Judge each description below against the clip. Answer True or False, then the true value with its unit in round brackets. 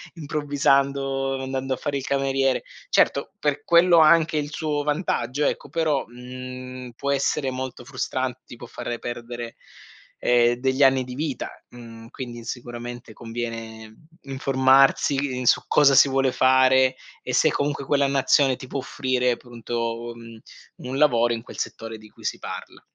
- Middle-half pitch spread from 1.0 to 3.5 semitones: True (2.5 semitones)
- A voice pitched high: False (130 Hz)